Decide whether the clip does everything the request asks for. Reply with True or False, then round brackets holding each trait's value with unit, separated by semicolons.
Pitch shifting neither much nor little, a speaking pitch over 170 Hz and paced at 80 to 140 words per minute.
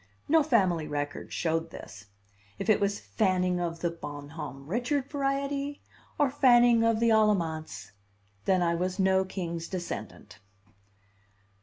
False (6.3 semitones; 185 Hz; 135 wpm)